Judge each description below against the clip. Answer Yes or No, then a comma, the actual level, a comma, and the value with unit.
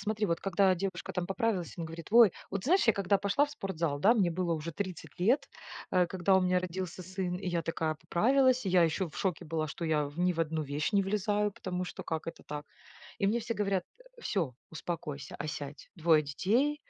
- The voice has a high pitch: No, medium, 180 Hz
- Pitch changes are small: No, average, 3.5 semitones